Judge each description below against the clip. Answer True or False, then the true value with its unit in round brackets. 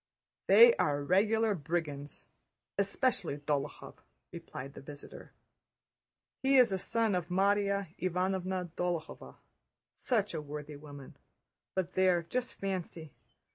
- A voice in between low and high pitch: True (180 Hz)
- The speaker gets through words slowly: True (110 wpm)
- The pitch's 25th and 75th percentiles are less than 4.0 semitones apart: False (4.8 semitones)